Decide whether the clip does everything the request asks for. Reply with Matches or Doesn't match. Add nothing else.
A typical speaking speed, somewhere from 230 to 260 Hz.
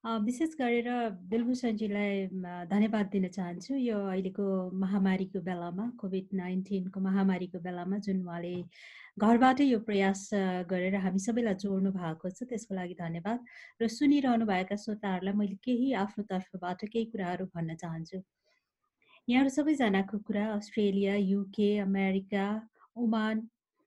Doesn't match